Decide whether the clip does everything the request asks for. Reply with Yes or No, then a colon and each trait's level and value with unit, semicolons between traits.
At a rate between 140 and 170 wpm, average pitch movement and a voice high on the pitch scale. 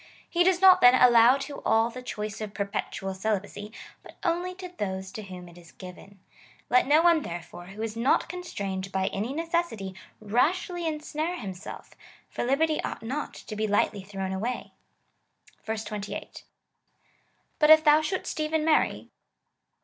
No: average, 155 wpm; wide, 7.9 semitones; high, 230 Hz